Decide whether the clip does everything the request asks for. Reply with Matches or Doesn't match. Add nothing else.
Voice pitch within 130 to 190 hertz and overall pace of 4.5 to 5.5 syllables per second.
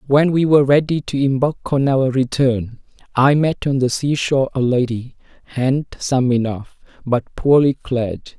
Matches